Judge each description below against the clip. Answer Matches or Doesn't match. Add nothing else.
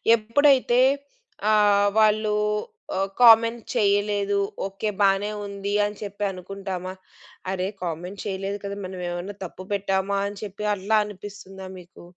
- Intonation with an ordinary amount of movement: Doesn't match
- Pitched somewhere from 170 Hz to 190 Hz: Doesn't match